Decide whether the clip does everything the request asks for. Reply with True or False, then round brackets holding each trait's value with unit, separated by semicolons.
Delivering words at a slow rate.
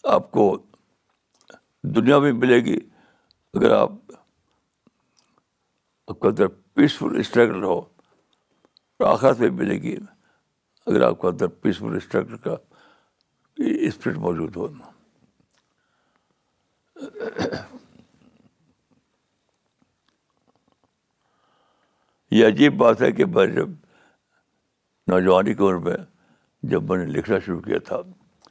True (95 wpm)